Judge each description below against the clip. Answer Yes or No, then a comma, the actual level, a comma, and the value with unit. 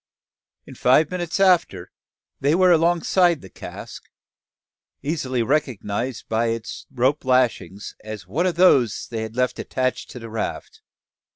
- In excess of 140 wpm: No, slow, 135 wpm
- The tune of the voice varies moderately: No, wide, 6.4 semitones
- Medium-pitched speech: No, low, 130 Hz